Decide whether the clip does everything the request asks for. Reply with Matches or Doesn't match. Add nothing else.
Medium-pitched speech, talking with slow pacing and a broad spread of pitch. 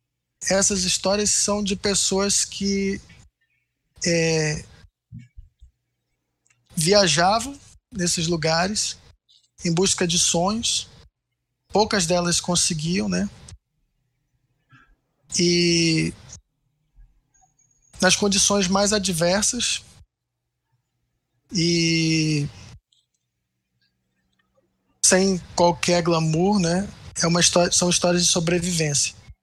Matches